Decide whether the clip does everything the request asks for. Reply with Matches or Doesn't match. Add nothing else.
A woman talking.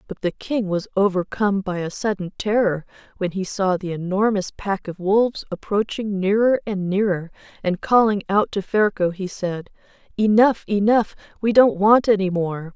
Matches